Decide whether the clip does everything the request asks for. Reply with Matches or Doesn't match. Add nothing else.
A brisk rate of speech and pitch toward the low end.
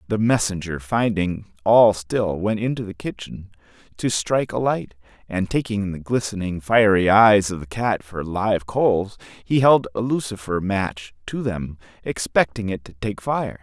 Doesn't match